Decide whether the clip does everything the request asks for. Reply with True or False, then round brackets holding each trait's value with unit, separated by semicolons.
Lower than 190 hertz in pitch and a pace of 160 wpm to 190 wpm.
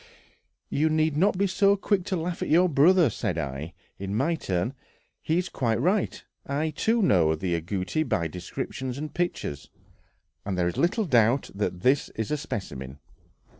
True (140 Hz; 170 wpm)